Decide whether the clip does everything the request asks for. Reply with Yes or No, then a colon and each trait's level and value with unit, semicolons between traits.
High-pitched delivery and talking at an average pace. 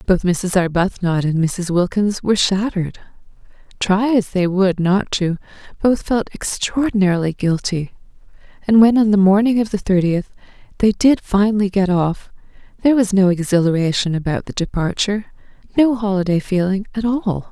Yes: high, 195 Hz; average, 145 wpm